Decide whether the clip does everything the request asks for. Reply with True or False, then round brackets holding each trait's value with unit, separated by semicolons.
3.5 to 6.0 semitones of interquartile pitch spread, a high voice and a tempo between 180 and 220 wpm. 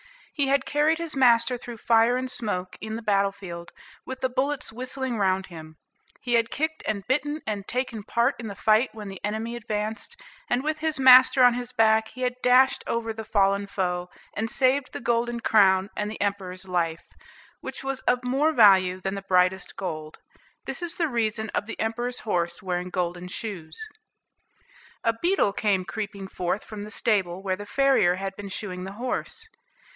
True (4.6 semitones; 220 Hz; 185 wpm)